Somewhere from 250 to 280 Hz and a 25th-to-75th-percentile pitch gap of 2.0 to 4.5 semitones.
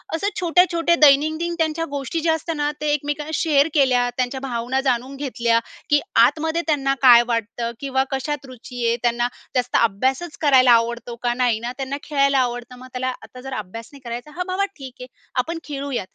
Yes: very high, 270 Hz; average, 3.8 semitones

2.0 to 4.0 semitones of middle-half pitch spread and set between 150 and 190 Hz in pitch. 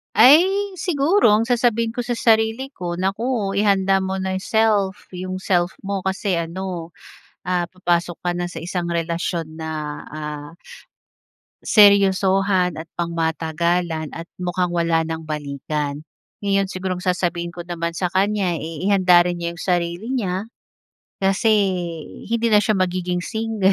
Yes: average, 2.9 semitones; medium, 185 Hz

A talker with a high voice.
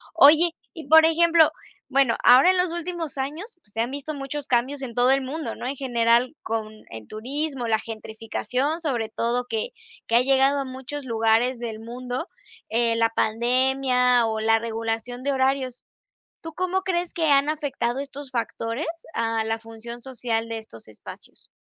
Yes: very high, 255 Hz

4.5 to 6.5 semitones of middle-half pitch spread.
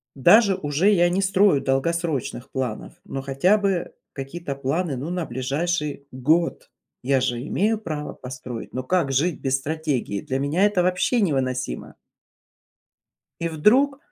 Yes: average, 5.2 semitones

